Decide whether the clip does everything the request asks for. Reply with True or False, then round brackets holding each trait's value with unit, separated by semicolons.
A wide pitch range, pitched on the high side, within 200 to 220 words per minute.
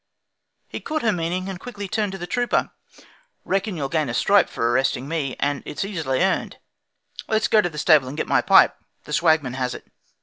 False (5.9 semitones; 170 Hz; 205 wpm)